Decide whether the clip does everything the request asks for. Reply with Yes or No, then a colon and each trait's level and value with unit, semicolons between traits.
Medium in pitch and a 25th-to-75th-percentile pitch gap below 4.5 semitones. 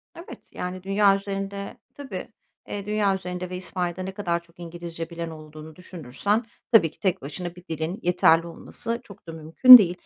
Yes: medium, 180 Hz; average, 3.0 semitones